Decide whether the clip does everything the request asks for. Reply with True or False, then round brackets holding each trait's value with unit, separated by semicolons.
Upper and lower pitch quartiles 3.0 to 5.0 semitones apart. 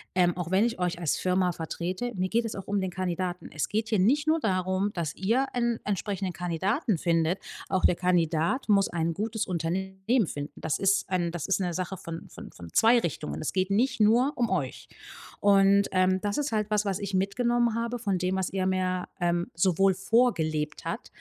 True (3.4 semitones)